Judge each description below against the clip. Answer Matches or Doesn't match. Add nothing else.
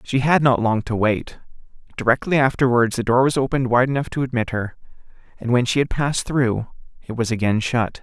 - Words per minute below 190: Doesn't match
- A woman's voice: Doesn't match